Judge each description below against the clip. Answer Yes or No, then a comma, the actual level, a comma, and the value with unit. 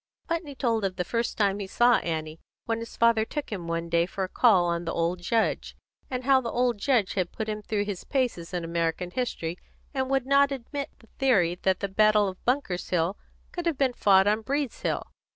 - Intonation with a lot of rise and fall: Yes, wide, 6.0 semitones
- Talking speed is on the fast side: Yes, fast, 215 wpm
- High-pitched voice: Yes, high, 215 Hz